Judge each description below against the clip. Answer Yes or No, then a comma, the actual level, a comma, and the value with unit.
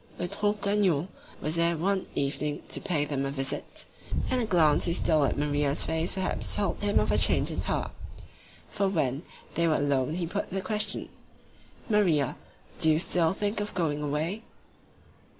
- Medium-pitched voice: Yes, medium, 165 Hz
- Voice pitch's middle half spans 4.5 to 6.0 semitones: Yes, average, 5.0 semitones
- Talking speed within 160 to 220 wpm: Yes, average, 170 wpm